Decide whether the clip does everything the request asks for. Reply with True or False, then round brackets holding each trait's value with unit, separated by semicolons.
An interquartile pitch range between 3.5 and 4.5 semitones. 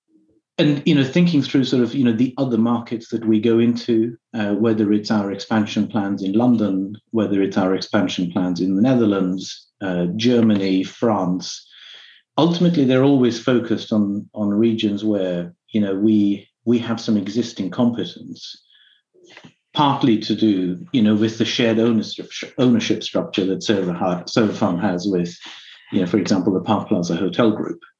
False (3.1 semitones)